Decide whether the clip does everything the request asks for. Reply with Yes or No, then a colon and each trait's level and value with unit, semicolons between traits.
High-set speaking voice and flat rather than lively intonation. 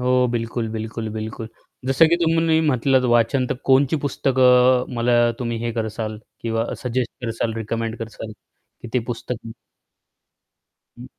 No: low, 120 Hz; narrow, 2.2 semitones